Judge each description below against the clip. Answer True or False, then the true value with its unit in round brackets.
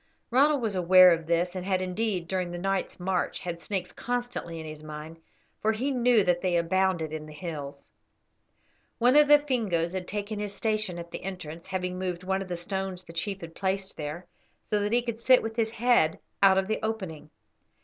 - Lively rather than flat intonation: False (4.1 semitones)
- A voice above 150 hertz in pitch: True (185 Hz)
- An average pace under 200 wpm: False (205 wpm)